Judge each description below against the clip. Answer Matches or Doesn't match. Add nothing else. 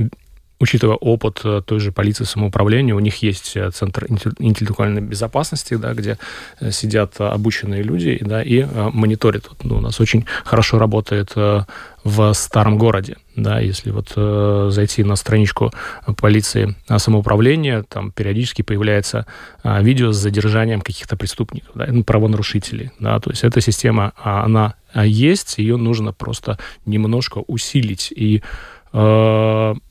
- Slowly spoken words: Doesn't match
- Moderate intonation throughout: Doesn't match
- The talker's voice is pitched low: Matches